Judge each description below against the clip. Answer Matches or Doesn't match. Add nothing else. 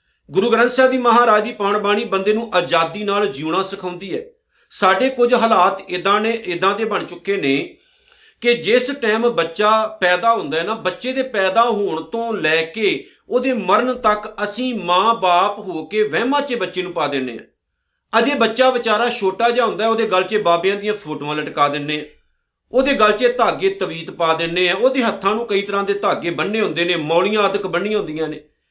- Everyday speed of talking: Doesn't match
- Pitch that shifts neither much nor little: Matches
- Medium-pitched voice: Doesn't match